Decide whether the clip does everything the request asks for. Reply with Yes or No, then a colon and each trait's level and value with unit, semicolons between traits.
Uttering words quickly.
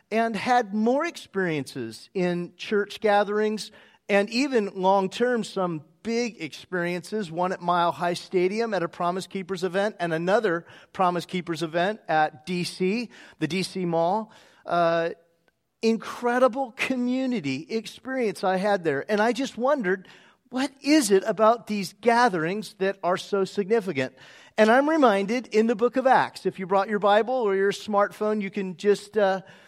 No: average, 150 wpm